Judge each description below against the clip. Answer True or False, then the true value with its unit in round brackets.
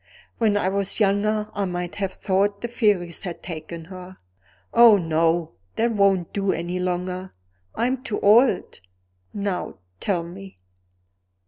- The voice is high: True (195 Hz)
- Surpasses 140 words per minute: False (135 wpm)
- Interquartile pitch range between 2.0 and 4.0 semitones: True (2.6 semitones)